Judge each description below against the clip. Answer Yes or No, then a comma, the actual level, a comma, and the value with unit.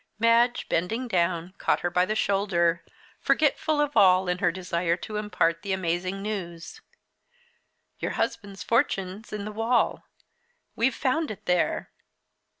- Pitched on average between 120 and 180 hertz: No, high, 195 Hz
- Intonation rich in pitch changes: No, average, 4.1 semitones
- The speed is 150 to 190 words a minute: No, average, 140 wpm